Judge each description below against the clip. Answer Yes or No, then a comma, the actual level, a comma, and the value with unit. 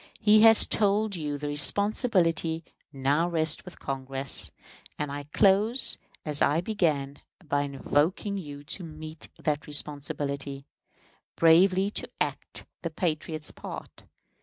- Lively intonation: No, average, 4.8 semitones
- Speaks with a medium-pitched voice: Yes, medium, 155 Hz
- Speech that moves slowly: Yes, slow, 120 wpm